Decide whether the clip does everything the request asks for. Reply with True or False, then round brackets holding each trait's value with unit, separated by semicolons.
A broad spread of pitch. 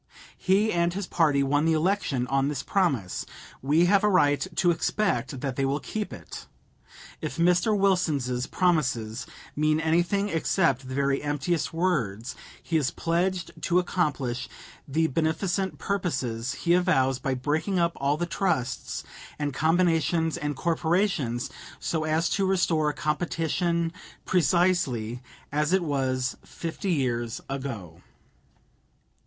False (4.7 semitones)